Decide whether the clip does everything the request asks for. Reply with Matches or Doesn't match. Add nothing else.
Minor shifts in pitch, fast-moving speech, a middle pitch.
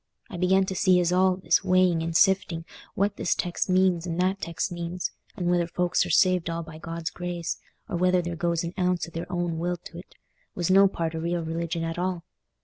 Matches